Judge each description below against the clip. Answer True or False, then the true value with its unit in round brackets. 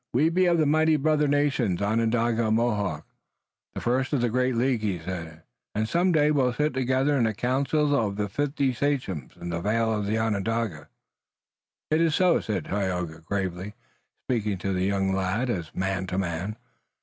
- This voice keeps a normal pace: True (185 wpm)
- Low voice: True (115 Hz)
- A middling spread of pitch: False (6.2 semitones)